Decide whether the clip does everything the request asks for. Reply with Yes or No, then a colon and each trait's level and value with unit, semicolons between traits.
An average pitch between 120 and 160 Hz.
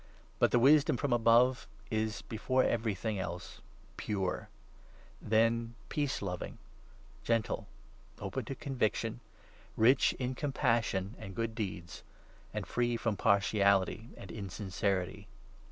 No: low, 110 Hz